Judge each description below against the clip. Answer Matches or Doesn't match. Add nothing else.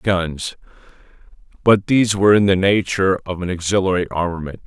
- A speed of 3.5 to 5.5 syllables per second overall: Doesn't match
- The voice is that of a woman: Doesn't match